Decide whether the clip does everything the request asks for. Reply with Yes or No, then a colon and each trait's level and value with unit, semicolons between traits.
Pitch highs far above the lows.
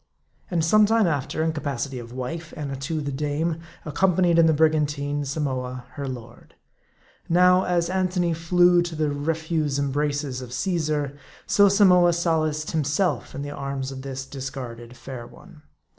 No: average, 3.7 semitones